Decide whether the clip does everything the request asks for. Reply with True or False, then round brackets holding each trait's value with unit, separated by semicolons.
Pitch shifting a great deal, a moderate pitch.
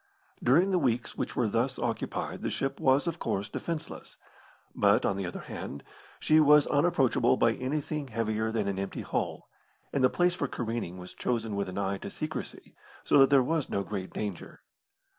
False (5.8 semitones; 120 Hz)